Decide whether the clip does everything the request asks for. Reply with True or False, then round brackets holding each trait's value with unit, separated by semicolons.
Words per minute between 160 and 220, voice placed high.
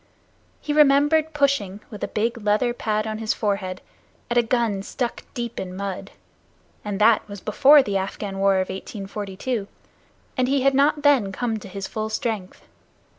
True (170 wpm; 215 Hz)